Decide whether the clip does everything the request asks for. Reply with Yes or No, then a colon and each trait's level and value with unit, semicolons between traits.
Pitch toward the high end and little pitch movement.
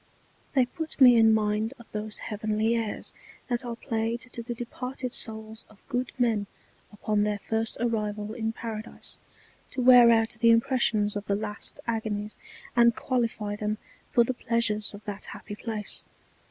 Yes: high, 225 Hz; narrow, 2.0 semitones